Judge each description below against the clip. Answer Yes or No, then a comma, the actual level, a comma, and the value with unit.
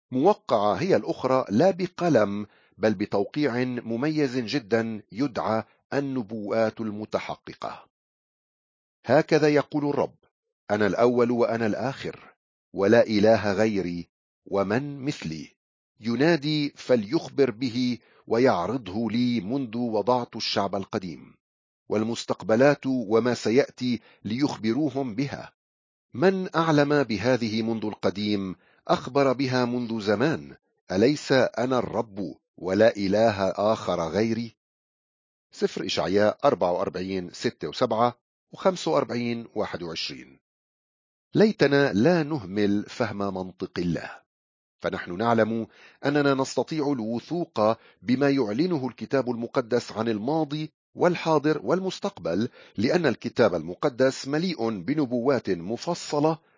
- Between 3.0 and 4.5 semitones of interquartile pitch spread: No, average, 5.3 semitones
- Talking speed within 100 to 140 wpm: No, average, 90 wpm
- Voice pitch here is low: Yes, low, 120 Hz